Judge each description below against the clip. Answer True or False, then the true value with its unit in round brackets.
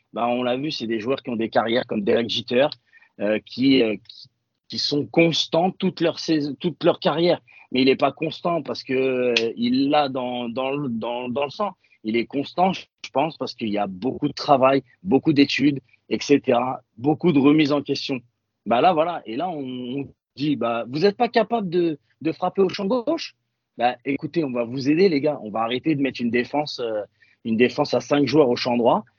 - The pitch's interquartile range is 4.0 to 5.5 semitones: True (4.8 semitones)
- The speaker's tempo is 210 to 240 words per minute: True (220 wpm)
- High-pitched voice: False (140 Hz)